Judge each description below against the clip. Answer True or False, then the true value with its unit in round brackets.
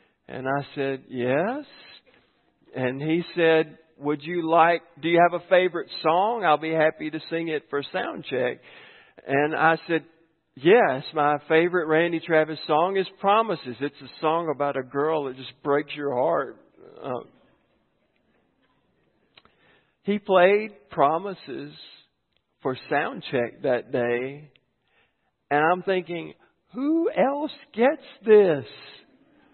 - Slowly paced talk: True (130 wpm)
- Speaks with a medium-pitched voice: True (160 Hz)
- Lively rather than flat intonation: False (4.8 semitones)